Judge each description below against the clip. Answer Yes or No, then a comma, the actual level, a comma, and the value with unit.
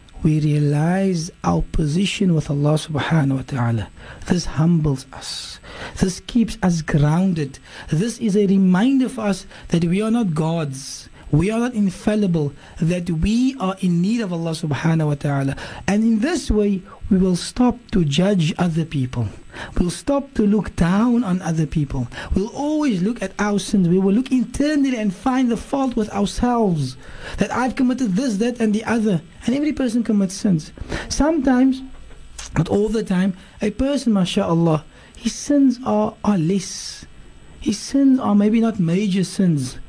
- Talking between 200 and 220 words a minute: No, average, 165 wpm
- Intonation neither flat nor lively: No, wide, 5.9 semitones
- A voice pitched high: Yes, high, 195 Hz